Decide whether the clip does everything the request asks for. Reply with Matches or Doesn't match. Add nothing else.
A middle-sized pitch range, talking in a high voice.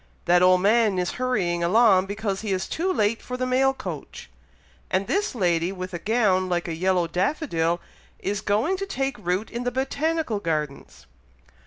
Doesn't match